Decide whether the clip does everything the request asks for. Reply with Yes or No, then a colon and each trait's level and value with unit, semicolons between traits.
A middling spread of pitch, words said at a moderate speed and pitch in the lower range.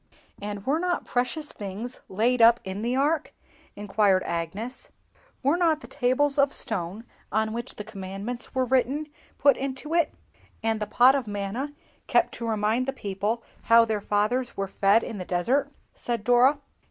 No: average, 4.5 semitones; average, 170 wpm; high, 235 Hz